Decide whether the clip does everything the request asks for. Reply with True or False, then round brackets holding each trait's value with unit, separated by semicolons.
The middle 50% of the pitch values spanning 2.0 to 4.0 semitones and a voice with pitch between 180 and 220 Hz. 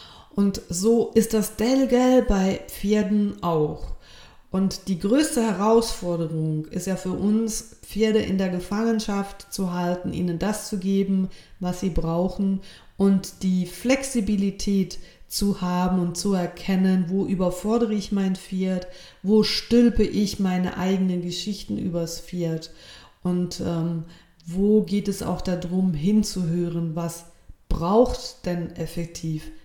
True (2.9 semitones; 190 Hz)